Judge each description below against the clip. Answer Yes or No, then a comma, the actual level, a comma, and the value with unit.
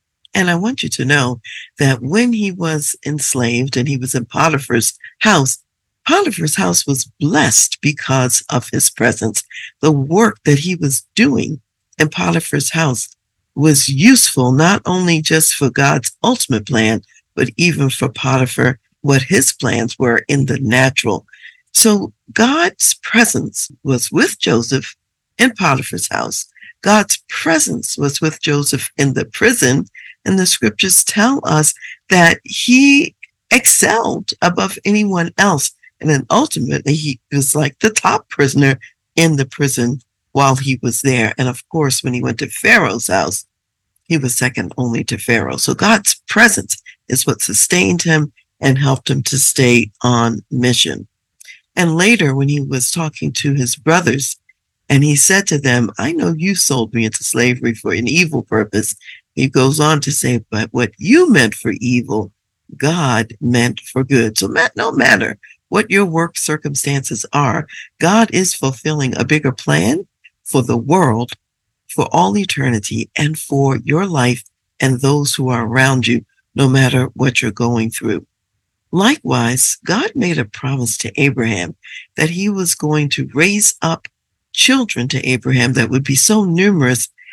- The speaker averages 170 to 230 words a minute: No, average, 155 wpm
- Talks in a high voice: No, low, 135 Hz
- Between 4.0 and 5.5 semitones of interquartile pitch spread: Yes, average, 4.7 semitones